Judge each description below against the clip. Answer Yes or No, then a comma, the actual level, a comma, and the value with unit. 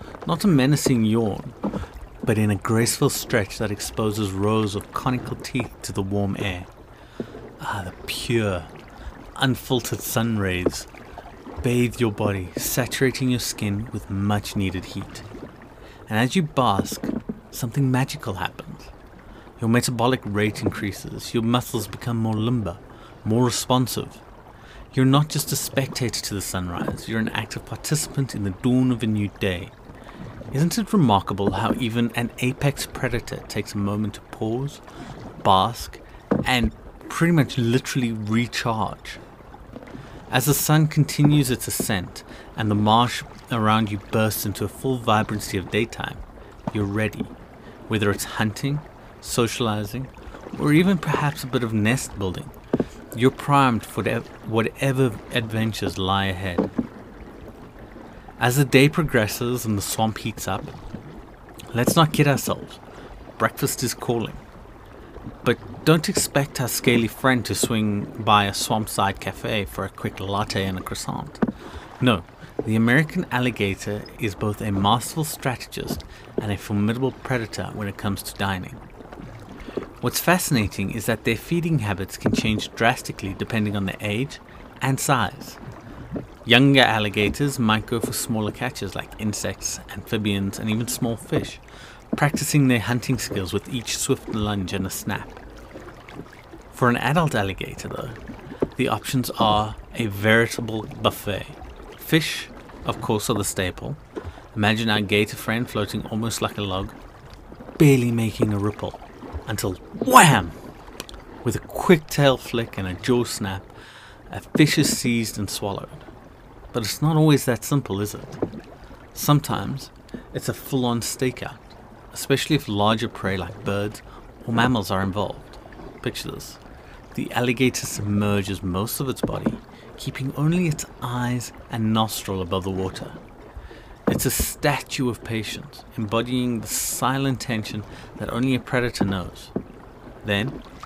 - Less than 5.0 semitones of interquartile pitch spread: Yes, average, 3.7 semitones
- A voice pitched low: Yes, low, 115 Hz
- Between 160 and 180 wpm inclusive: No, average, 140 wpm